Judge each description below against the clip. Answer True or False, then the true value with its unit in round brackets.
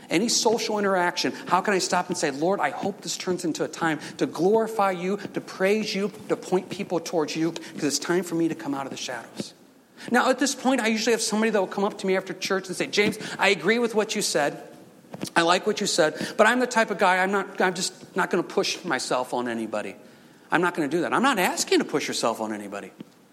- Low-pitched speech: False (190 Hz)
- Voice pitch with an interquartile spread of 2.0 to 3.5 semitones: False (3.9 semitones)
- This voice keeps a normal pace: False (255 wpm)